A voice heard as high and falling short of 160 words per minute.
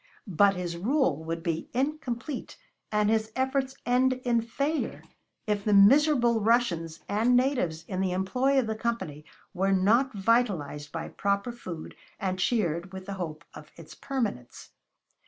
Yes: high, 210 Hz; average, 150 wpm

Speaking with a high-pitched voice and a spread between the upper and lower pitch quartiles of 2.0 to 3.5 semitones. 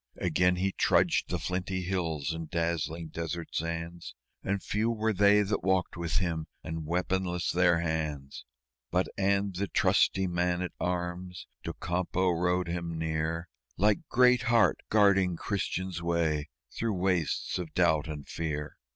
No: very low, 90 Hz; narrow, 2.4 semitones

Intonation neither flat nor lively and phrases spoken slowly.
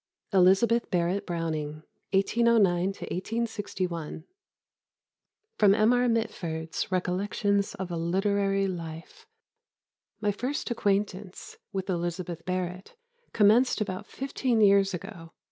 Yes: average, 3.2 semitones; slow, 95 wpm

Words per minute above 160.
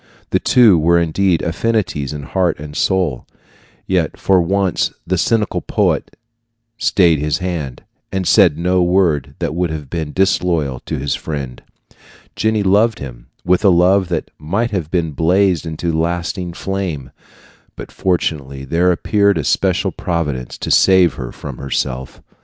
No: average, 150 wpm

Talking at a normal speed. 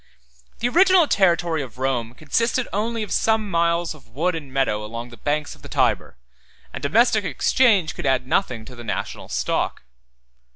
Yes: average, 170 wpm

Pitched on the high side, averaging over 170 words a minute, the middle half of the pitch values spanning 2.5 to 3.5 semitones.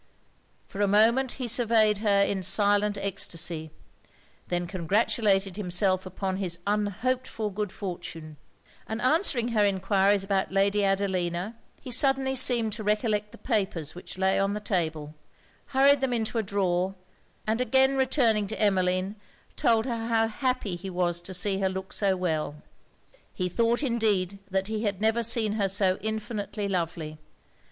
No: high, 205 Hz; average, 155 wpm; average, 3.1 semitones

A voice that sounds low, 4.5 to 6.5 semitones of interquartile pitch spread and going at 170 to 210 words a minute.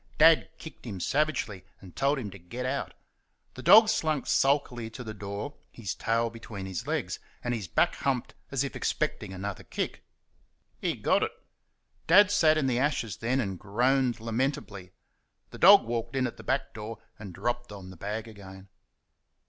Yes: low, 115 Hz; average, 5.3 semitones; average, 175 wpm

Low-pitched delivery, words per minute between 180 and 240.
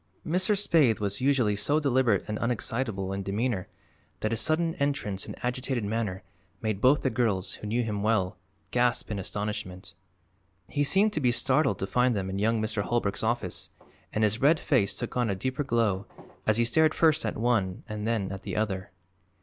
Yes: low, 115 Hz; average, 190 wpm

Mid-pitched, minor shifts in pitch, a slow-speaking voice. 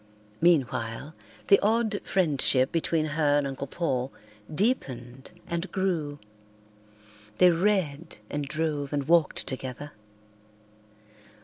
No: medium, 150 Hz; average, 3.9 semitones; slow, 100 wpm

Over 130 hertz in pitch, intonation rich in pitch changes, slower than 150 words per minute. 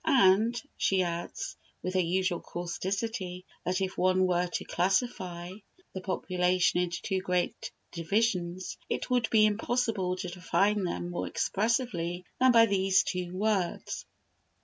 No: medium, 185 Hz; average, 2.8 semitones; slow, 135 wpm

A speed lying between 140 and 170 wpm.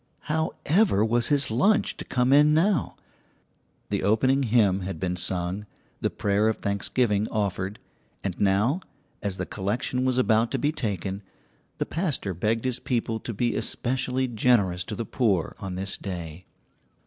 Yes: average, 160 wpm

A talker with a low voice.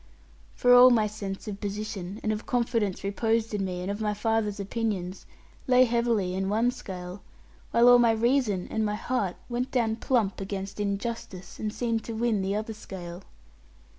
No: high, 215 Hz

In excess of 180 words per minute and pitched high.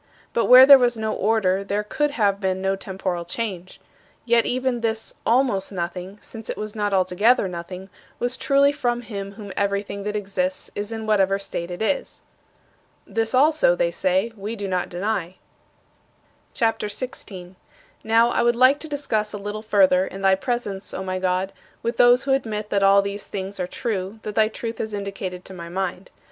Yes: average, 190 wpm; high, 210 Hz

